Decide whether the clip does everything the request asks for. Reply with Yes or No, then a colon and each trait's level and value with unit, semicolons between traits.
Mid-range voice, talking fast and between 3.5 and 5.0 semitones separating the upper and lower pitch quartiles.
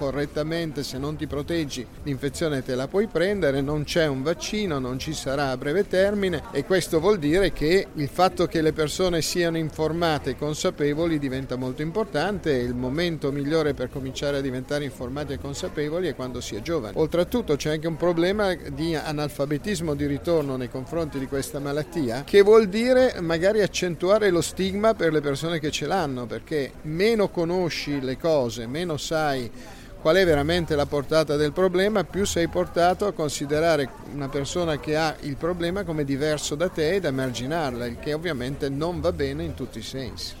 Yes: medium, 155 Hz; fast, 180 wpm; average, 3.8 semitones